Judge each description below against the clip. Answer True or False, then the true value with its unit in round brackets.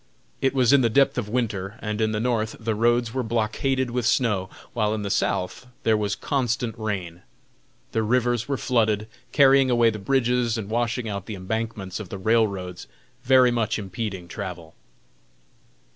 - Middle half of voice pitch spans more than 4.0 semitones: False (2.9 semitones)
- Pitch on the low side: True (110 Hz)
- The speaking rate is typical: True (170 wpm)